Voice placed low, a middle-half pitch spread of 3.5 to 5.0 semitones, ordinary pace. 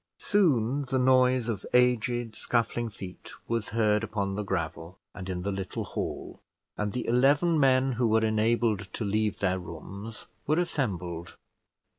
Yes: low, 110 Hz; average, 4.2 semitones; average, 150 wpm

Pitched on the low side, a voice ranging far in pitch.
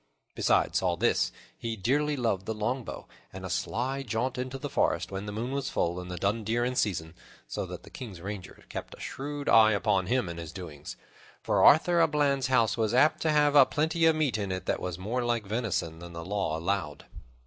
Yes: low, 110 Hz; wide, 6.1 semitones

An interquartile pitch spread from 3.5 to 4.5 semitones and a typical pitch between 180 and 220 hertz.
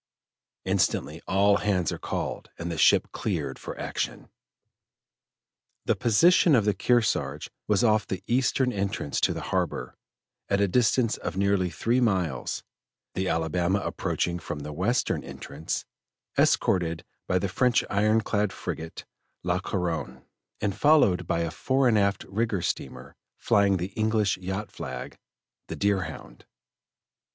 No: average, 3.8 semitones; low, 100 Hz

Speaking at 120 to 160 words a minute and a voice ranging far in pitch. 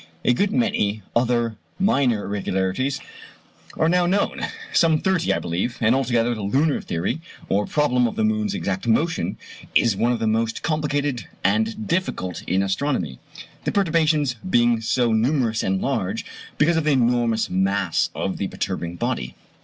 Yes: average, 155 wpm; wide, 6.4 semitones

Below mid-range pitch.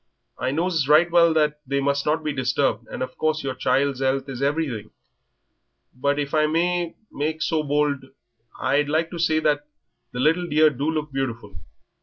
No: medium, 145 Hz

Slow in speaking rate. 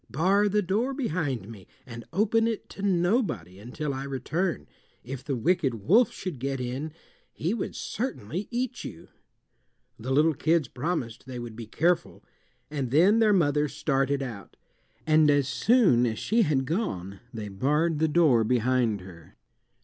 No: average, 155 wpm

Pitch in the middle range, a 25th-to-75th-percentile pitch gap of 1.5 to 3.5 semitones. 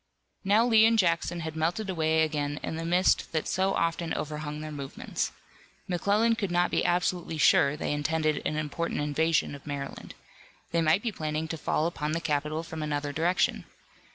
Yes: medium, 160 Hz; narrow, 2.6 semitones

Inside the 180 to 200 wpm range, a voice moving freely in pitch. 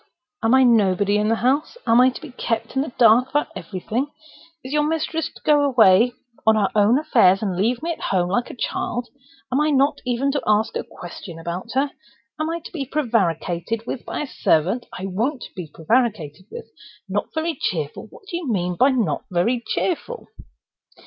Yes: average, 195 wpm; wide, 6.1 semitones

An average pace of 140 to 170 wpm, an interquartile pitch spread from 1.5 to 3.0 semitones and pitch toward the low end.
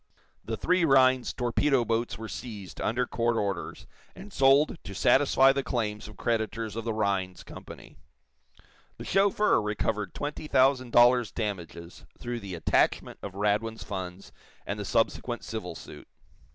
No: average, 145 wpm; average, 4.2 semitones; low, 115 Hz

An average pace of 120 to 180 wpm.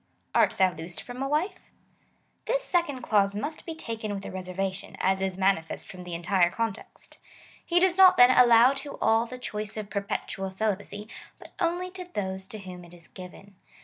No: average, 190 wpm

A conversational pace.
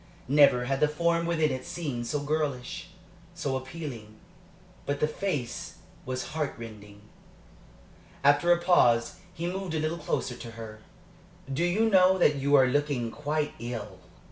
Yes: average, 150 wpm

